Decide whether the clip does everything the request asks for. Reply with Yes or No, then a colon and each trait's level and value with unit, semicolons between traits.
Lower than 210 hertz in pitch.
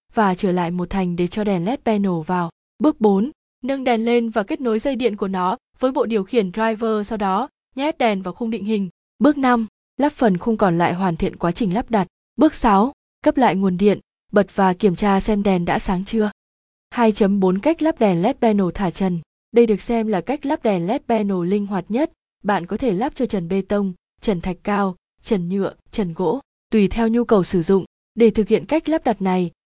No: high, 215 Hz